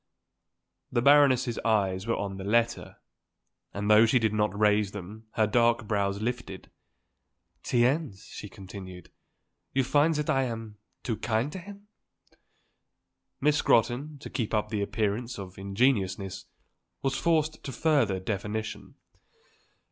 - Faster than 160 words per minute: No, slow, 135 wpm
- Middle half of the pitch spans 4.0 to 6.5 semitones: Yes, average, 4.4 semitones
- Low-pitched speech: Yes, low, 110 Hz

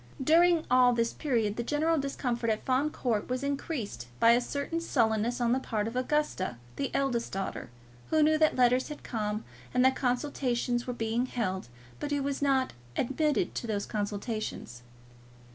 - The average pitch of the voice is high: Yes, very high, 250 Hz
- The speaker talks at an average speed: Yes, average, 170 wpm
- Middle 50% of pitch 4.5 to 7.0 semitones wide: No, average, 3.9 semitones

